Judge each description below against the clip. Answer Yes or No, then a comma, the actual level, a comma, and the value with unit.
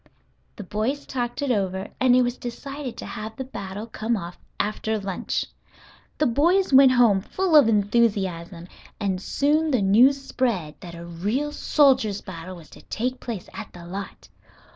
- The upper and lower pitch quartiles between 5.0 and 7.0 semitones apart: Yes, average, 5.3 semitones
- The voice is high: Yes, high, 220 Hz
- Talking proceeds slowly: No, average, 165 wpm